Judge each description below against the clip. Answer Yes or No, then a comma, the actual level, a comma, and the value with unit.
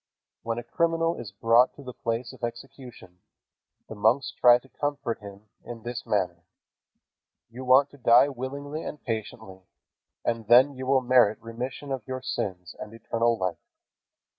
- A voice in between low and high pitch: No, low, 120 Hz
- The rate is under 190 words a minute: Yes, average, 160 wpm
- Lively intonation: No, average, 3.0 semitones